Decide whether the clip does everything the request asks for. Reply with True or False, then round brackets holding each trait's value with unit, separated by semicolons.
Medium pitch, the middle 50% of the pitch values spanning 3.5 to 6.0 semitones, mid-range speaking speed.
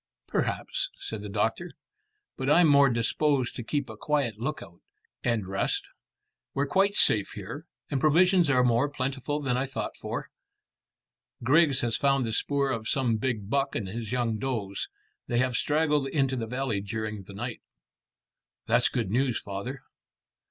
False (125 Hz; 4.2 semitones; 160 wpm)